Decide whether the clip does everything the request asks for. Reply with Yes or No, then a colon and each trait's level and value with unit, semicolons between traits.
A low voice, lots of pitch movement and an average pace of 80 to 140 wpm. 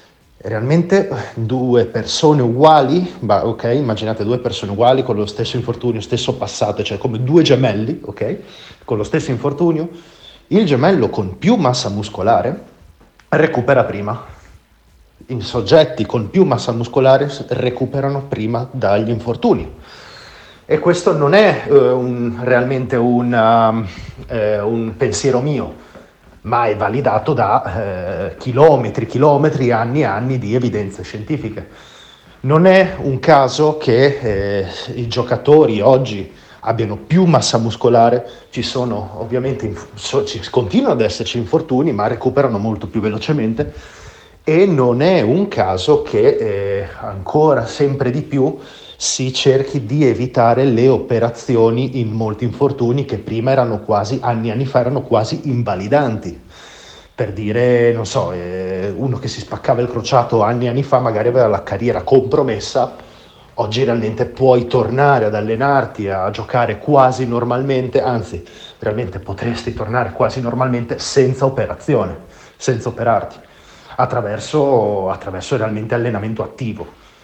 No: low, 120 Hz; average, 3.5 semitones; average, 130 wpm